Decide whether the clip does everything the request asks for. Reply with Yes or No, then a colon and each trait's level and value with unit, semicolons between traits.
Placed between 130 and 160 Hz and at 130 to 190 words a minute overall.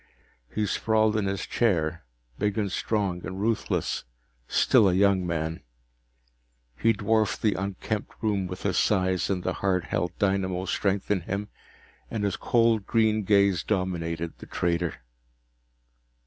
No: low, 100 Hz; average, 140 wpm